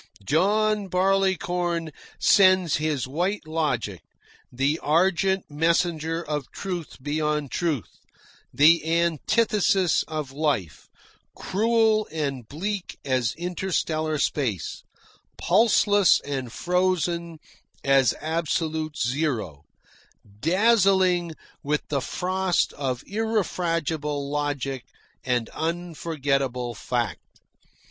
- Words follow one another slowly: Yes, slow, 85 wpm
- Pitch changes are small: No, average, 4.5 semitones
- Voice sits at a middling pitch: Yes, medium, 160 Hz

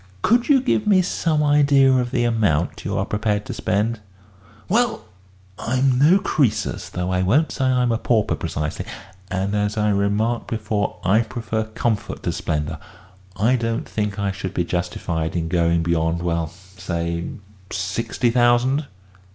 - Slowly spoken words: No, average, 155 wpm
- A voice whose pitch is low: Yes, low, 105 Hz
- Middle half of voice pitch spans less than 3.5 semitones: No, wide, 5.6 semitones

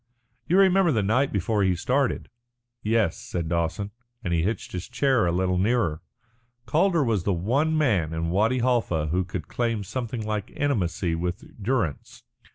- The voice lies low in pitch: Yes, low, 105 Hz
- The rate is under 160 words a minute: No, average, 165 wpm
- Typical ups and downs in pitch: No, wide, 6.2 semitones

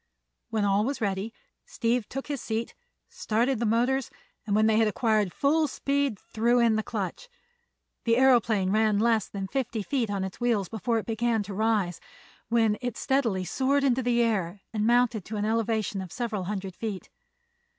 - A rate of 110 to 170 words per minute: No, average, 180 wpm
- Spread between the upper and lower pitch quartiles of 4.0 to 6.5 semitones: No, average, 2.8 semitones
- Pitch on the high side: Yes, high, 225 Hz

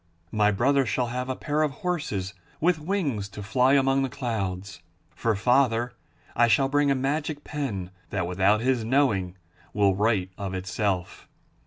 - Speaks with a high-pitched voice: No, low, 120 Hz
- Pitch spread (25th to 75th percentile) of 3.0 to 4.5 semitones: No, wide, 5.5 semitones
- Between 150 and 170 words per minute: Yes, average, 160 wpm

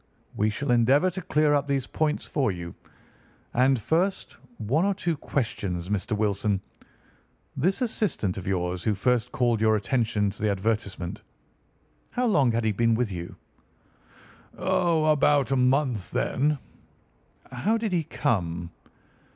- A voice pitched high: No, low, 120 Hz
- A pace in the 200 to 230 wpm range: No, slow, 135 wpm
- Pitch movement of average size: No, wide, 6.6 semitones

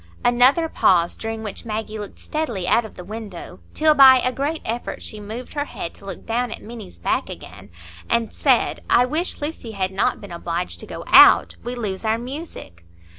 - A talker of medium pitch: No, high, 225 Hz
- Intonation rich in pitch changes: No, average, 4.4 semitones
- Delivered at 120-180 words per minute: No, average, 195 wpm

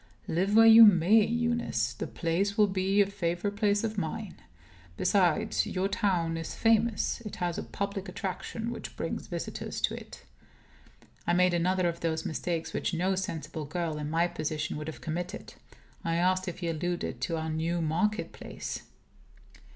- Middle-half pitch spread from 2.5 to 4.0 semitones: Yes, average, 3.7 semitones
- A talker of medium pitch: Yes, medium, 180 Hz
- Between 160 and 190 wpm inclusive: Yes, average, 165 wpm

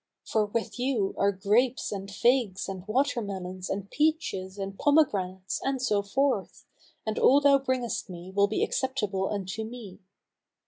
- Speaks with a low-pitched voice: No, high, 210 Hz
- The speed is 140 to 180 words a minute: Yes, average, 150 wpm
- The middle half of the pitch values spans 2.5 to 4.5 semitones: No, average, 5.1 semitones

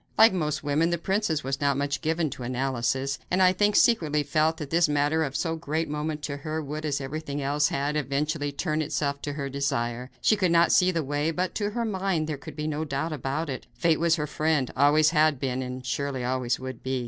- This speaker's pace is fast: Yes, fast, 230 wpm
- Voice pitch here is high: No, medium, 150 Hz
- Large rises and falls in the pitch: No, narrow, 2.6 semitones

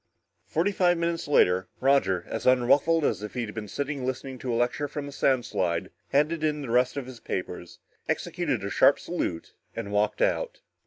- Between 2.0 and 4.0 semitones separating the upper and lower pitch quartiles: No, wide, 5.6 semitones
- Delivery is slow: No, average, 195 wpm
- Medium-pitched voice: No, low, 130 Hz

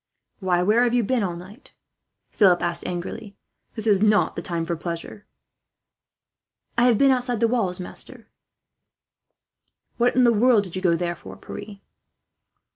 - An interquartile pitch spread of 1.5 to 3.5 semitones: No, average, 5.0 semitones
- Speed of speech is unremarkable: Yes, average, 170 wpm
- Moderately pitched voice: No, high, 205 Hz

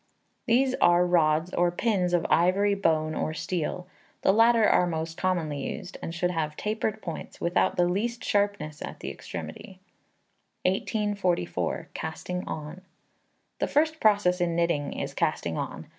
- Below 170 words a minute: Yes, average, 145 wpm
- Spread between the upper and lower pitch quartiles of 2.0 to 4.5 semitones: Yes, average, 3.8 semitones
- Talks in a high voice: No, medium, 180 Hz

